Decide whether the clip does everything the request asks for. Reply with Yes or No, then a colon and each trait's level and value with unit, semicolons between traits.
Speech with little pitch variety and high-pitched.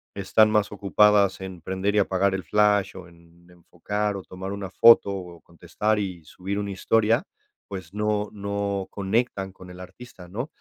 No: narrow, 2.2 semitones; low, 100 Hz